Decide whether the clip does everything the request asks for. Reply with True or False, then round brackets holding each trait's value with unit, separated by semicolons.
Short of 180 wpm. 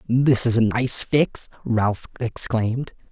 True (135 wpm)